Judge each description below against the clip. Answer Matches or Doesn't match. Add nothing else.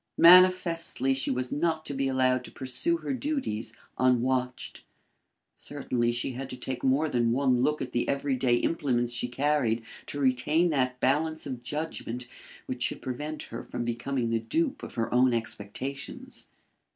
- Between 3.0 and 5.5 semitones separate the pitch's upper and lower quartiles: Matches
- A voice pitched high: Doesn't match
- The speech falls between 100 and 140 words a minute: Doesn't match